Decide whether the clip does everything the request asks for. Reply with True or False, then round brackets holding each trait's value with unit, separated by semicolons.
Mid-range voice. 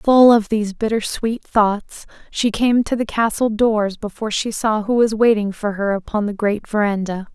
False (215 Hz)